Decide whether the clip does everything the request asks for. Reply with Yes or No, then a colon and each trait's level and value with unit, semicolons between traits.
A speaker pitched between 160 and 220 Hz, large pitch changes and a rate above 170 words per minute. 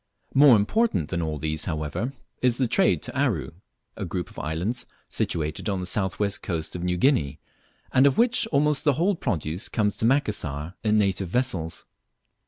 No: low, 100 Hz; wide, 8.3 semitones; average, 180 wpm